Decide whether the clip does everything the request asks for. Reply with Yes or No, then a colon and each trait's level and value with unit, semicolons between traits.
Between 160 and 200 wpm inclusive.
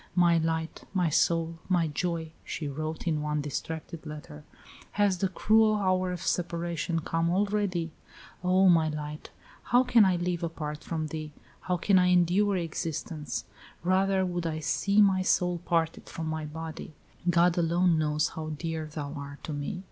Yes: average, 165 wpm